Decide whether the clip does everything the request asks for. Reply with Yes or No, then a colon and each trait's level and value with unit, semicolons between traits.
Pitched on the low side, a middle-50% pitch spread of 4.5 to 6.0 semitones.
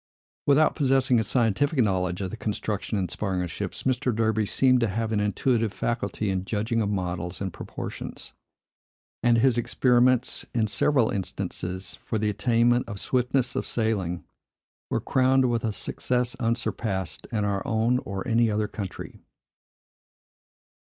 No: low, 110 Hz; average, 3.7 semitones